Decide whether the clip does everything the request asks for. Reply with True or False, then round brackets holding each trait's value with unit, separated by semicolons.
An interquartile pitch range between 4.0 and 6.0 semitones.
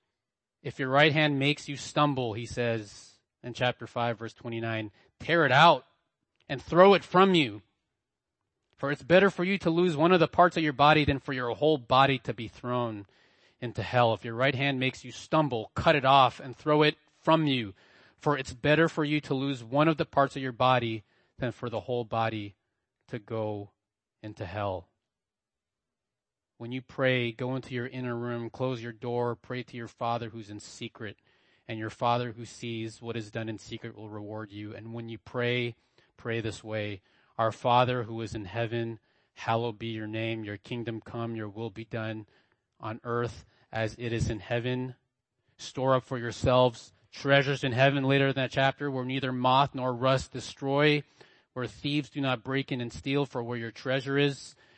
False (3.2 semitones)